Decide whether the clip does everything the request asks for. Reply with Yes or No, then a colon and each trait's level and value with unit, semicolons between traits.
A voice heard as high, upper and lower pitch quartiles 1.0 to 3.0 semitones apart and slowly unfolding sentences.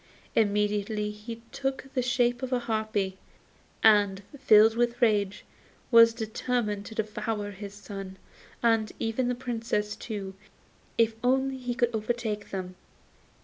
Yes: high, 220 Hz; narrow, 2.6 semitones; slow, 130 wpm